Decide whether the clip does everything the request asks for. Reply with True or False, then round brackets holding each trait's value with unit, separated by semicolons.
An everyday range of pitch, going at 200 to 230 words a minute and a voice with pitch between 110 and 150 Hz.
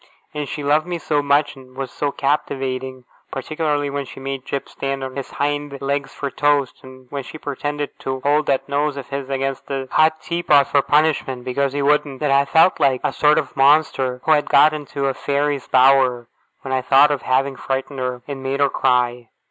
False (1.7 semitones; 205 wpm; 140 Hz)